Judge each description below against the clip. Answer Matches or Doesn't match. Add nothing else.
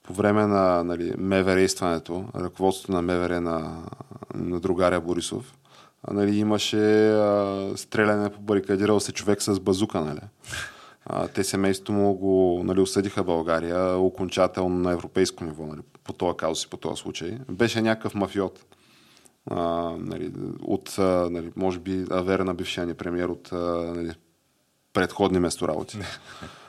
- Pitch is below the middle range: Matches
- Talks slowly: Doesn't match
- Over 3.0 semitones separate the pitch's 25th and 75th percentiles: Doesn't match